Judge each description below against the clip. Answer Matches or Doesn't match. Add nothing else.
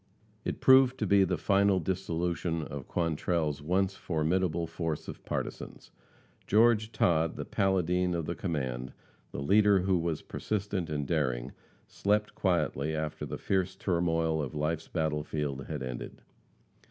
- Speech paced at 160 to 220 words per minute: Doesn't match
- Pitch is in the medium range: Doesn't match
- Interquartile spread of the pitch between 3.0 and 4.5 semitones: Matches